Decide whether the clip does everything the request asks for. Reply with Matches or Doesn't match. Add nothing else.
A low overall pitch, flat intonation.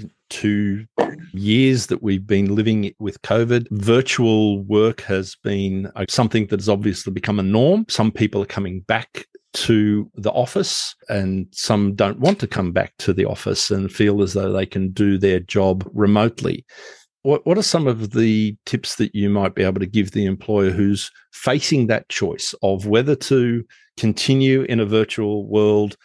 Matches